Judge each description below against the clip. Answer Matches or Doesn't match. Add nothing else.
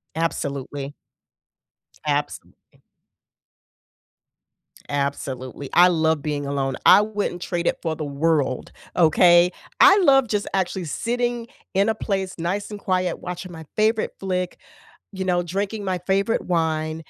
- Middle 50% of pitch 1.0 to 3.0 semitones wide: Doesn't match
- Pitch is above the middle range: Doesn't match